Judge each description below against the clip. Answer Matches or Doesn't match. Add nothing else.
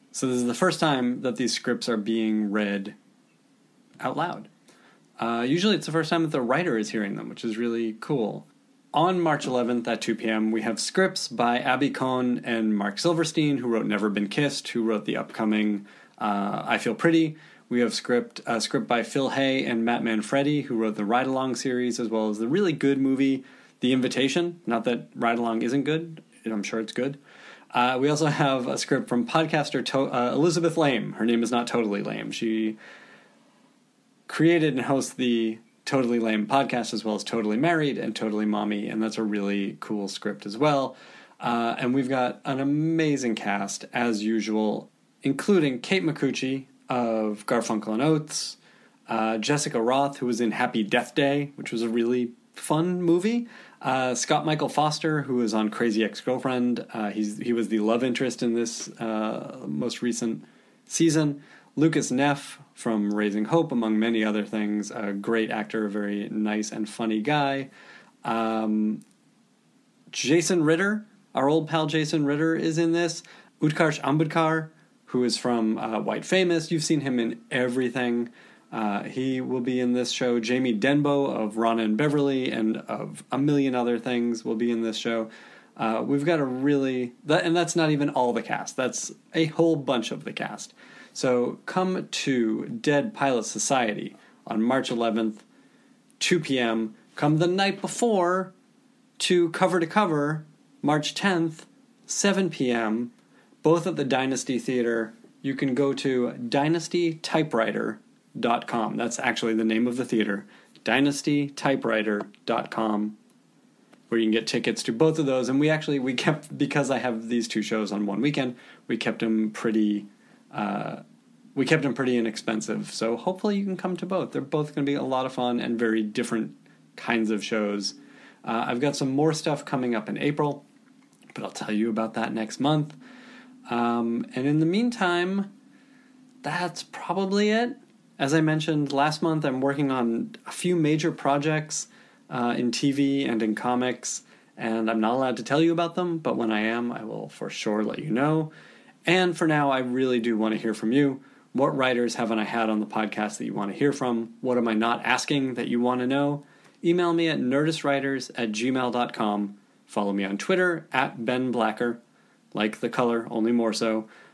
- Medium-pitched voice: Doesn't match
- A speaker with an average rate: Matches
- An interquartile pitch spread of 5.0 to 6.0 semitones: Matches